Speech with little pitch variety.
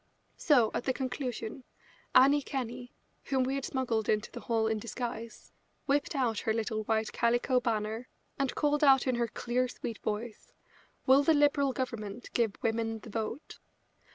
No: average, 3.1 semitones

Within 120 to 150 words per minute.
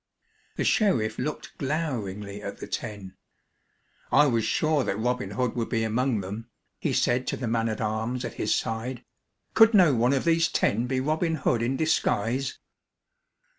No: average, 170 wpm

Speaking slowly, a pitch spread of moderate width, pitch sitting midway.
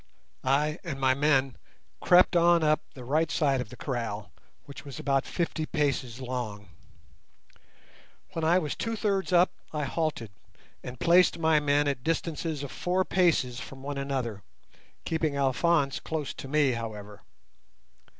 No: average, 150 wpm; average, 4.0 semitones; medium, 145 Hz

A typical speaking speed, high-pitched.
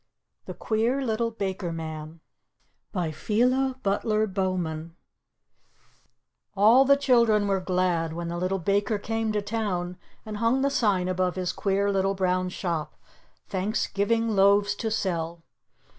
No: slow, 130 wpm; high, 195 Hz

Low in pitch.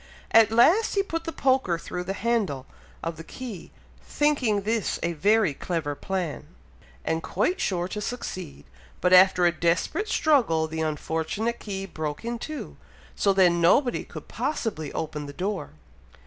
No: high, 190 Hz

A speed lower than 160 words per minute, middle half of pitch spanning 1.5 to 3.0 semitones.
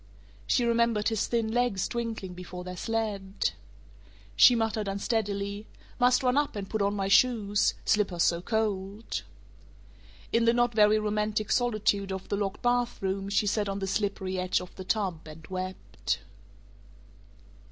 Yes: average, 150 wpm; average, 2.7 semitones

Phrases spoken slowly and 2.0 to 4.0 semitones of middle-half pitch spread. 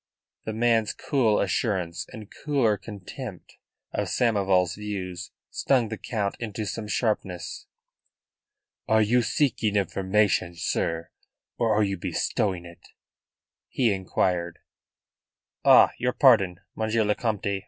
Yes: slow, 115 wpm; average, 3.0 semitones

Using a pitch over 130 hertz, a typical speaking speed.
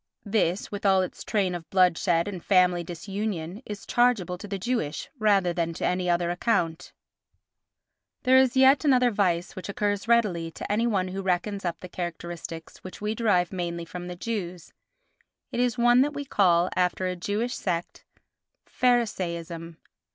Yes: medium, 185 Hz; average, 165 wpm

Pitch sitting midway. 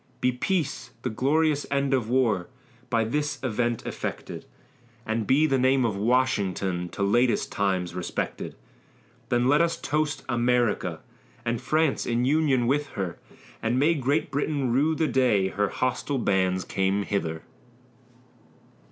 No: low, 125 Hz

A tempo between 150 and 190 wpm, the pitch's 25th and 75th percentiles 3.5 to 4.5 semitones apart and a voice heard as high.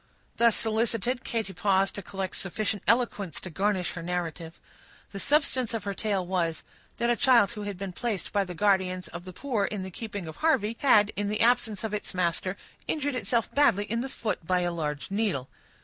No: average, 200 wpm; average, 3.9 semitones; high, 205 Hz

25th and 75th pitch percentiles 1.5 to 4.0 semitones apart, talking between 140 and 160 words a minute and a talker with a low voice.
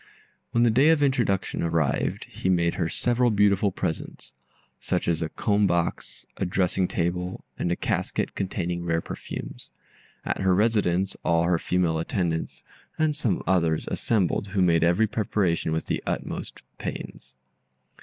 Yes: average, 3.6 semitones; average, 150 wpm; very low, 90 Hz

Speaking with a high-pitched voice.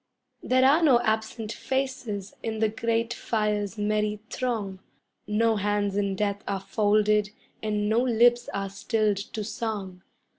Yes: high, 215 Hz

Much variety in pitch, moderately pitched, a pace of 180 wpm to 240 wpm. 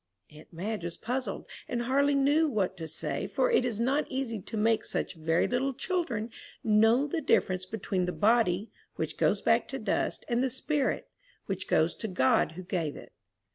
No: wide, 6.2 semitones; high, 225 Hz; average, 185 wpm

